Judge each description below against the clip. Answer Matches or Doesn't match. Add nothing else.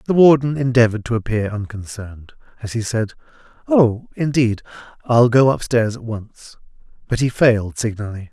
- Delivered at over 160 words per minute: Doesn't match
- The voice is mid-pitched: Doesn't match